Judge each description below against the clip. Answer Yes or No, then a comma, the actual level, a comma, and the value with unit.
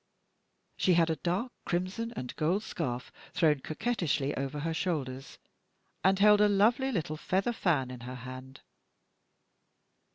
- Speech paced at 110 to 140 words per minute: Yes, slow, 135 wpm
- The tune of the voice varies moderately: No, wide, 6.6 semitones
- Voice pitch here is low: No, medium, 165 Hz